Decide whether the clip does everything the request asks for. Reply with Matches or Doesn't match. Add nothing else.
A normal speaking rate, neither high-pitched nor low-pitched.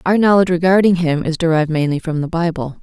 Doesn't match